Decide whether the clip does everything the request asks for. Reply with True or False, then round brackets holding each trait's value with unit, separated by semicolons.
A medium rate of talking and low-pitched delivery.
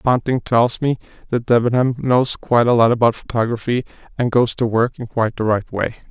True (195 wpm; 120 Hz)